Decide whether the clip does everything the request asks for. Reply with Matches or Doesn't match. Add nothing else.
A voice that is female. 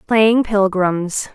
Matches